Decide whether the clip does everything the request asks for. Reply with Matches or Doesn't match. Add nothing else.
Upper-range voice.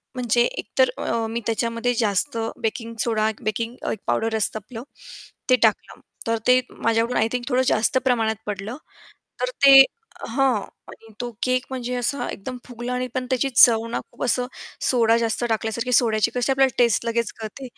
Matches